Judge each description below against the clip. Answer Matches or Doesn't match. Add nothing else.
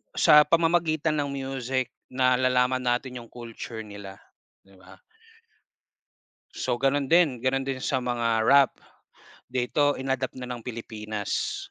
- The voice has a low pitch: Matches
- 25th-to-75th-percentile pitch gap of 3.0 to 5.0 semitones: Doesn't match